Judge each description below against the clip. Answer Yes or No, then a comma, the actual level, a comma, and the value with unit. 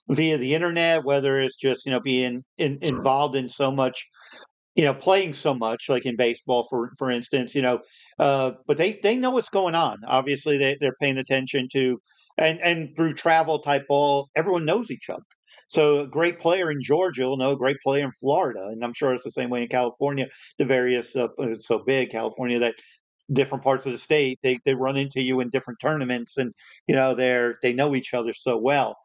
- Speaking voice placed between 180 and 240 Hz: No, low, 135 Hz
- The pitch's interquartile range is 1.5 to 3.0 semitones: Yes, average, 2.7 semitones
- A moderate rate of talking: No, fast, 215 wpm